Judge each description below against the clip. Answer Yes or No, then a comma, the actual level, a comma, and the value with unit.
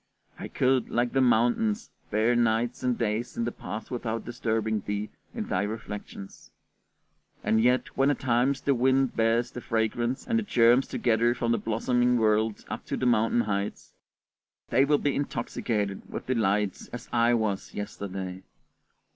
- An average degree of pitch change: No, narrow, 2.3 semitones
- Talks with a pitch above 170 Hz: No, low, 115 Hz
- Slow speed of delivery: No, average, 160 wpm